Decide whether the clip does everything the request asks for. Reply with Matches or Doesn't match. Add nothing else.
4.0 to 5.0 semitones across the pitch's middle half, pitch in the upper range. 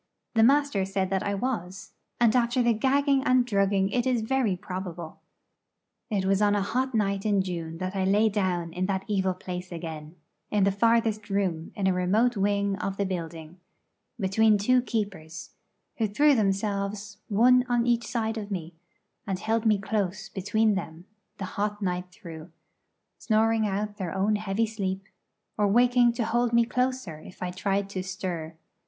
Doesn't match